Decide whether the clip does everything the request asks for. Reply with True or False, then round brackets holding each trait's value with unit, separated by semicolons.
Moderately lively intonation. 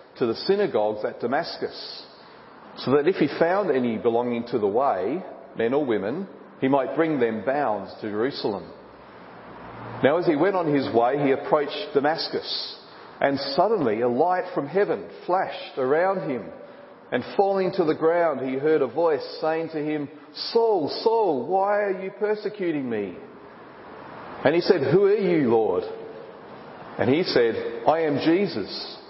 False (8.5 semitones)